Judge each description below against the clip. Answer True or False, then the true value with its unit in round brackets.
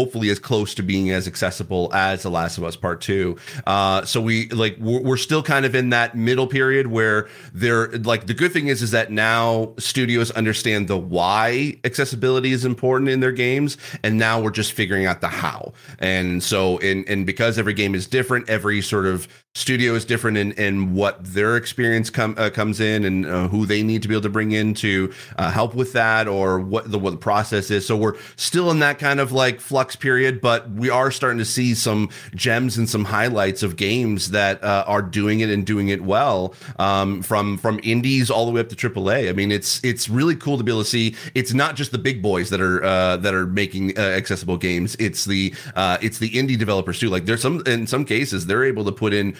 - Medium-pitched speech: False (110 Hz)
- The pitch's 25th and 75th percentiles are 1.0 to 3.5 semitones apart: False (3.9 semitones)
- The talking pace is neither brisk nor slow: False (230 wpm)